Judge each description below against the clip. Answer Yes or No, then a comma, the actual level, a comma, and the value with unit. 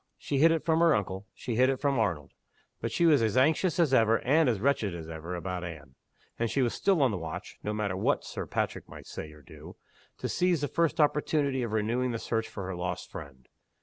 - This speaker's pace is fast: Yes, fast, 235 wpm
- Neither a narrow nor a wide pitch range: No, wide, 7.8 semitones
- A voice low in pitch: Yes, low, 115 Hz